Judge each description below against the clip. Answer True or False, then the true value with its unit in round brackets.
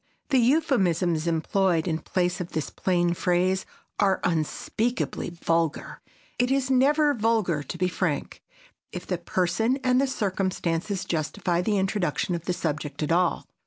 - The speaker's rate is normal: True (145 wpm)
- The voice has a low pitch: False (180 Hz)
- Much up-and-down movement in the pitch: False (4.7 semitones)